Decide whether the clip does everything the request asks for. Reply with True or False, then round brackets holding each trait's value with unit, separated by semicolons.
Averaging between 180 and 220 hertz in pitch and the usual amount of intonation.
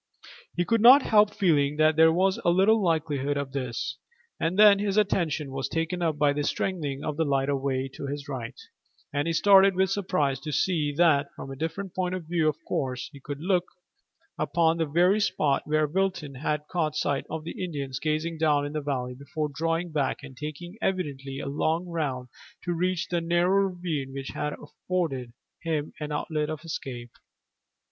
False (155 Hz; 3.8 semitones)